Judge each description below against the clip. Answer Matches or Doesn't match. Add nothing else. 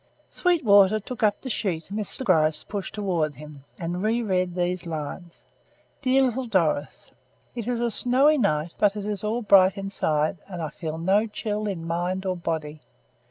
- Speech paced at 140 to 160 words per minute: Doesn't match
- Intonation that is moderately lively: Matches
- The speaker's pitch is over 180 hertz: Matches